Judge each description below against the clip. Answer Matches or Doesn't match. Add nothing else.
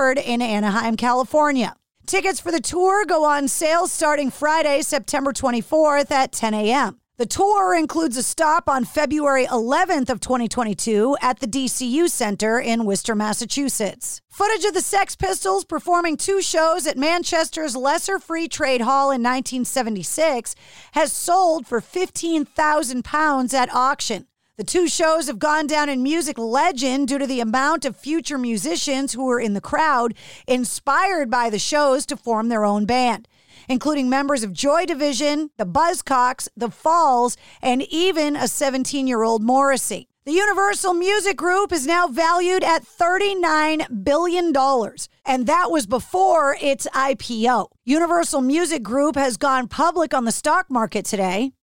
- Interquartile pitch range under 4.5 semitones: Doesn't match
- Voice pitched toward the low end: Doesn't match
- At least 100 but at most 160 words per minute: Matches